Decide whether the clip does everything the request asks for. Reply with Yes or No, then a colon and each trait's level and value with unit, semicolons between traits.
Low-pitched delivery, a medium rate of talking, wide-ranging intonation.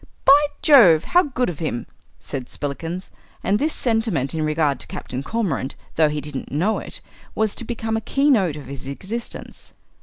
No: medium, 180 Hz; average, 175 wpm; wide, 7.8 semitones